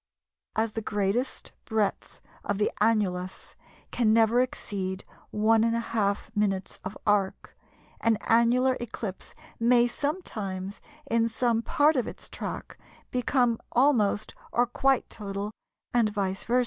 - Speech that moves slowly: Yes, slow, 120 wpm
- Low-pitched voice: No, high, 225 Hz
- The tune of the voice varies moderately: Yes, average, 3.0 semitones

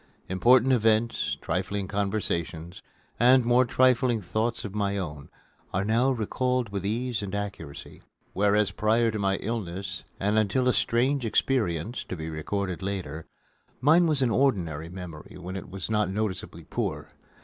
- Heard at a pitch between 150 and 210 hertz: No, low, 105 Hz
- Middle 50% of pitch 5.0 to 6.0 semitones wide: No, average, 4.2 semitones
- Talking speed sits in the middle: Yes, average, 150 wpm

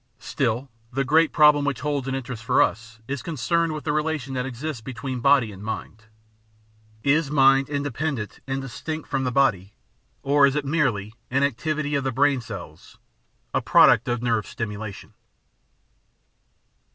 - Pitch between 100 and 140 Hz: Yes, low, 135 Hz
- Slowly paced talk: No, average, 160 wpm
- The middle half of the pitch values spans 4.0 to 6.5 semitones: No, average, 3.6 semitones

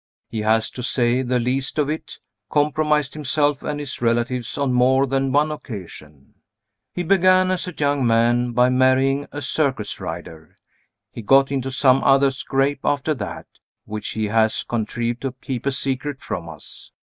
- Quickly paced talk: No, average, 165 wpm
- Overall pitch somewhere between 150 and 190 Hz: No, low, 130 Hz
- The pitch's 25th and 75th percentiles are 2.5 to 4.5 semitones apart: Yes, average, 3.3 semitones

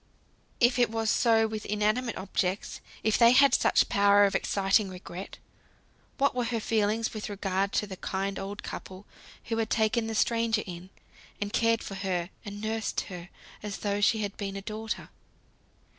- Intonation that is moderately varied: No, narrow, 2.3 semitones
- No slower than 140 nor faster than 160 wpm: No, average, 175 wpm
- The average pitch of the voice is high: Yes, high, 210 Hz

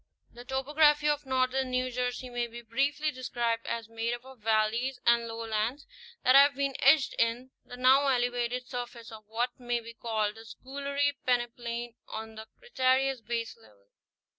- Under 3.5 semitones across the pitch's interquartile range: Yes, narrow, 2.4 semitones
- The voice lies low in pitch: No, high, 245 Hz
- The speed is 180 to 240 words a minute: No, average, 165 wpm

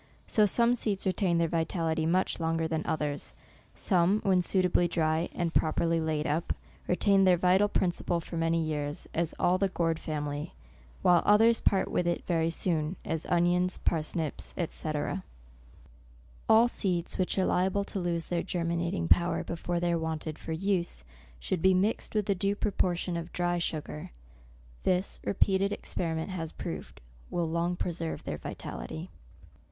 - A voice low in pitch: No, medium, 170 Hz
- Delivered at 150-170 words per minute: Yes, average, 160 wpm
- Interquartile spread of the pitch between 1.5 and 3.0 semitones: Yes, narrow, 2.4 semitones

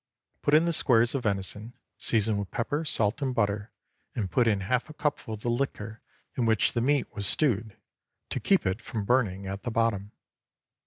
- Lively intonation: No, average, 3.9 semitones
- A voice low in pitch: Yes, low, 115 Hz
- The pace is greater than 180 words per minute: Yes, average, 195 wpm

